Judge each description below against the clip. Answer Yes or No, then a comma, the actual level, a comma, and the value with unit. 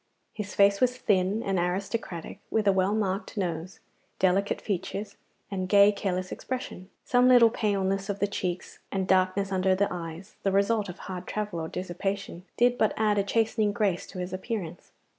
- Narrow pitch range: Yes, narrow, 2.1 semitones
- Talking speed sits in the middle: Yes, average, 175 wpm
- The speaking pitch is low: No, high, 195 Hz